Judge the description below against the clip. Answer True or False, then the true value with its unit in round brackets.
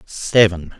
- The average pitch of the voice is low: True (95 Hz)